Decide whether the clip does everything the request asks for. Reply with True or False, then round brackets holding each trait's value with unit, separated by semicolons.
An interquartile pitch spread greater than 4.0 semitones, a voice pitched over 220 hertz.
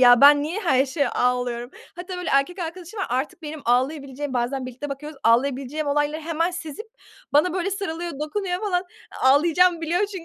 True (4.7 semitones; 300 Hz)